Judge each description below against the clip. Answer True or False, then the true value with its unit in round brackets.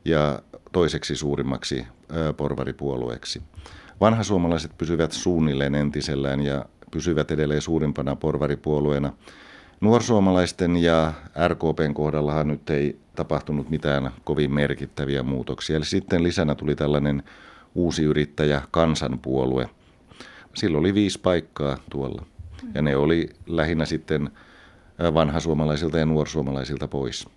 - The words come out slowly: False (105 wpm)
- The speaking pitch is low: True (75 Hz)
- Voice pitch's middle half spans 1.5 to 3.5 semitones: True (2.5 semitones)